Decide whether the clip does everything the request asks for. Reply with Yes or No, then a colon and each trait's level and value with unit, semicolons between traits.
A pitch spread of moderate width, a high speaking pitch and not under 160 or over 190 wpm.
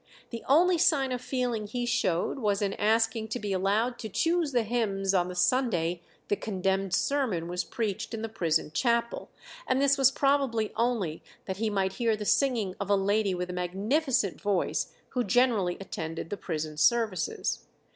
Yes: average, 4.5 semitones; high, 215 Hz; average, 175 wpm